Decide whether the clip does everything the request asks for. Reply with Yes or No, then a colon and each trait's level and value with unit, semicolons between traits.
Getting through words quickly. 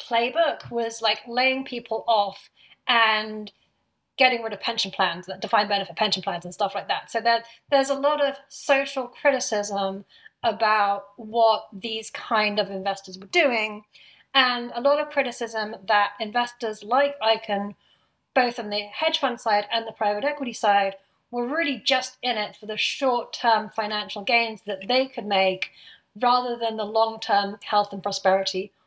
No: average, 165 wpm